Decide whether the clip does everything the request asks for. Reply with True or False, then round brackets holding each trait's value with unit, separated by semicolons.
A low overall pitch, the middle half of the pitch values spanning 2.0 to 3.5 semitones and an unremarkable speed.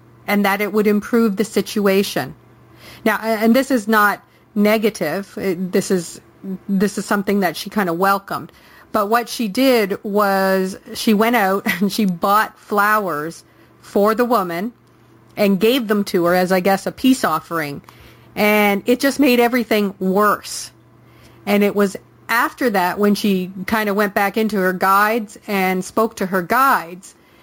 False (205 Hz; 3.1 semitones; 160 wpm)